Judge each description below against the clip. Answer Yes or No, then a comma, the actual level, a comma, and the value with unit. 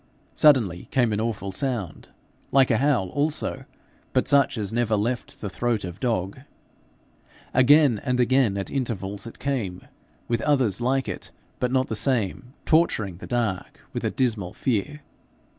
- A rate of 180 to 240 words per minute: No, average, 155 wpm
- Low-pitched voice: Yes, low, 120 Hz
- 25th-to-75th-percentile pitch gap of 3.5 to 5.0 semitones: Yes, average, 4.5 semitones